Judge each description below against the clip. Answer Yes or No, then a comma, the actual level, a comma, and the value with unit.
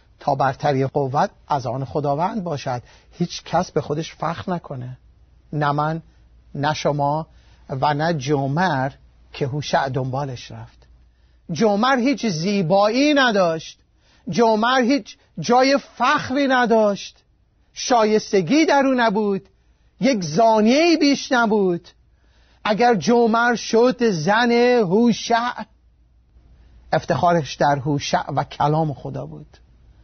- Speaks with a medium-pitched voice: Yes, medium, 170 Hz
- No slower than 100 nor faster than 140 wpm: Yes, slow, 105 wpm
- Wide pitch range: Yes, wide, 8.6 semitones